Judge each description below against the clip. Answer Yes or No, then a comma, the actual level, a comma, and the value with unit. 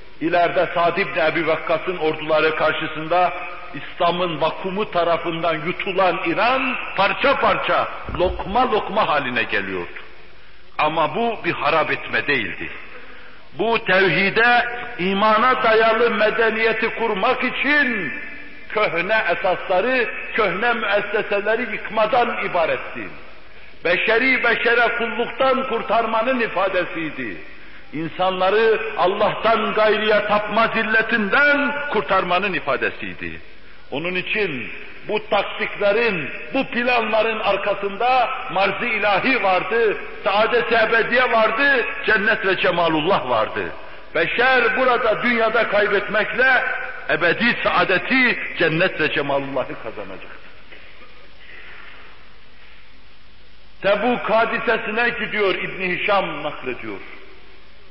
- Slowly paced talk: Yes, slow, 85 wpm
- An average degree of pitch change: Yes, average, 4.4 semitones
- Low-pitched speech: No, high, 210 Hz